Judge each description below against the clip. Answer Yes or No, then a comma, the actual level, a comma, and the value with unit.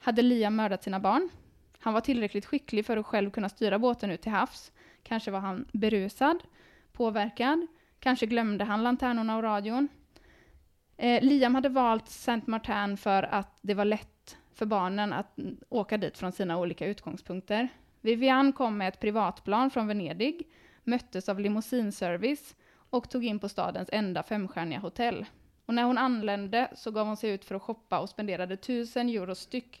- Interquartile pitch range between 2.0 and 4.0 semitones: Yes, average, 3.3 semitones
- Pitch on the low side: No, high, 220 Hz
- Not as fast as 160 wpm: No, average, 170 wpm